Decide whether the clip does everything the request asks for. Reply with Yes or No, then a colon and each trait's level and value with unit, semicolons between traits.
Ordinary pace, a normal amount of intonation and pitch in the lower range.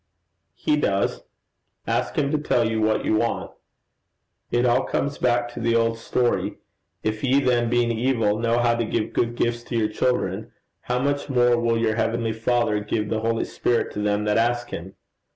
No: average, 190 wpm; narrow, 1.8 semitones; low, 115 Hz